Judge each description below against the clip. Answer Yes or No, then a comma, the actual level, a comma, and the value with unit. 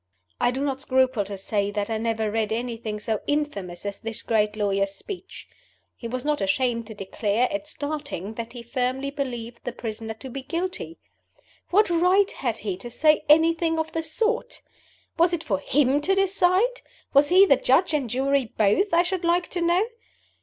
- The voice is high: Yes, very high, 260 Hz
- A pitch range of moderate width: No, wide, 6.8 semitones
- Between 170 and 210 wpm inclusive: Yes, average, 185 wpm